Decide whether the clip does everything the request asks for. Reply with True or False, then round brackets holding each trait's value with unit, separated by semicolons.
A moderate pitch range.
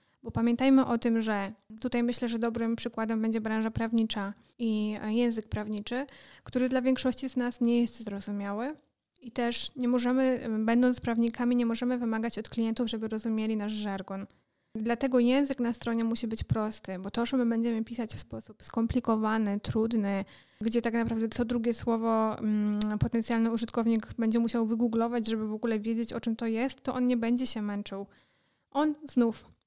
False (1.6 semitones)